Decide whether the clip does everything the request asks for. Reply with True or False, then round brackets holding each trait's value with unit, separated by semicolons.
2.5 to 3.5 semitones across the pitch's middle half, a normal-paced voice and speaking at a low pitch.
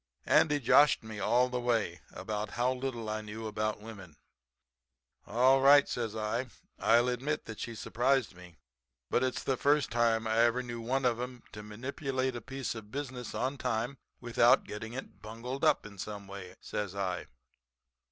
True (3.2 semitones; 170 wpm; 120 Hz)